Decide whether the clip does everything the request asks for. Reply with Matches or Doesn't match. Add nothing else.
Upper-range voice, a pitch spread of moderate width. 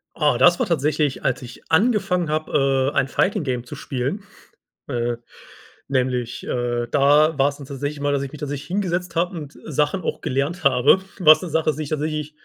Doesn't match